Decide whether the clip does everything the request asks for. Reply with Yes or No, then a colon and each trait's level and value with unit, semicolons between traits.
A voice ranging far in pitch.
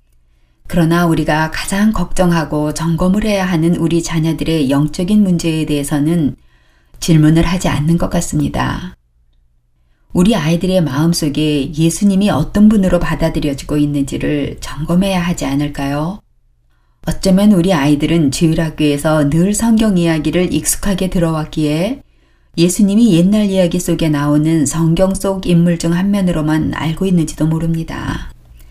No: average, 3.4 semitones